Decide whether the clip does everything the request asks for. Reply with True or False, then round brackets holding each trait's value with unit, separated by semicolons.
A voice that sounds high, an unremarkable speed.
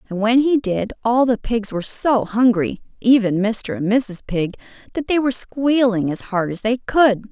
True (225 Hz; 195 wpm)